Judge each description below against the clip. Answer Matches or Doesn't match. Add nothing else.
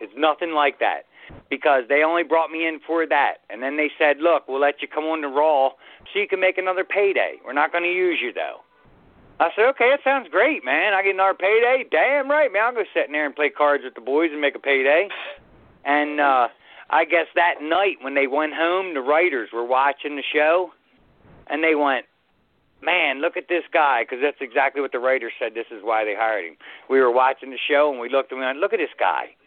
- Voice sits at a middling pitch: Matches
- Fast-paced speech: Matches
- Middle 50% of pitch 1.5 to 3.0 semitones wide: Doesn't match